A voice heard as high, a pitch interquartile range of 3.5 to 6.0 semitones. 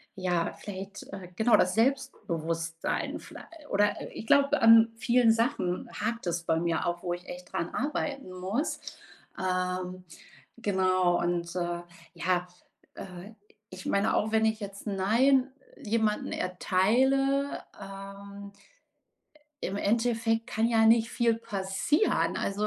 Yes: high, 200 Hz; average, 3.9 semitones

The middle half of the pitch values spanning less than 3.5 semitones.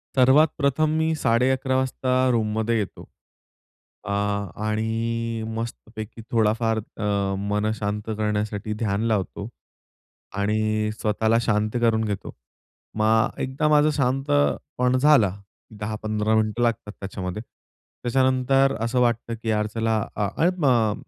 Yes: average, 3.0 semitones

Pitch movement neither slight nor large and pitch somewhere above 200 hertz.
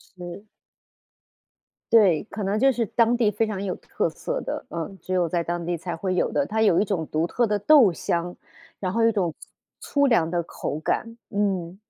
No: average, 4.5 semitones; high, 195 Hz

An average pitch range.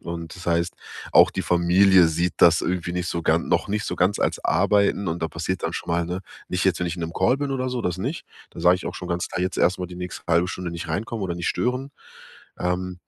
No: narrow, 1.9 semitones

